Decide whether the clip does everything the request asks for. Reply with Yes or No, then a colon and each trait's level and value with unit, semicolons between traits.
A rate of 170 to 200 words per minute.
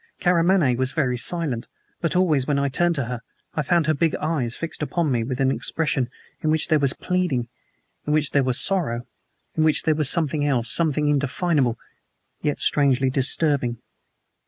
Yes: average, 180 wpm